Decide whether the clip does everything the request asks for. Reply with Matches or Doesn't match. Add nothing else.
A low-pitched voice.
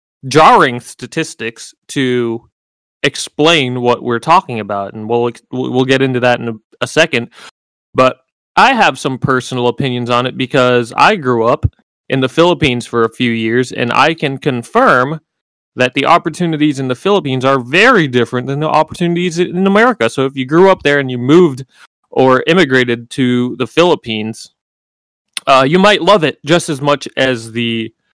Matches